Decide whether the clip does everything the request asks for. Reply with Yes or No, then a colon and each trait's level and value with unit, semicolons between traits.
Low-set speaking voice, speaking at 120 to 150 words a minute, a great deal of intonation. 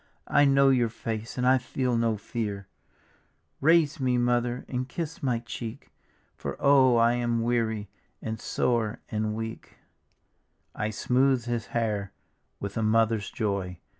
No: low, 115 Hz; average, 140 wpm; narrow, 2.5 semitones